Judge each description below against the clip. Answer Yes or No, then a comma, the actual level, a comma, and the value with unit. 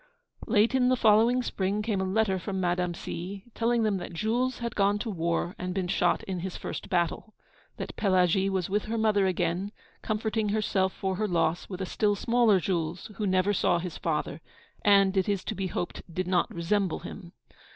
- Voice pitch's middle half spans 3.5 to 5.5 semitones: No, average, 3.0 semitones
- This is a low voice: No, high, 195 Hz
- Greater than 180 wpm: Yes, average, 200 wpm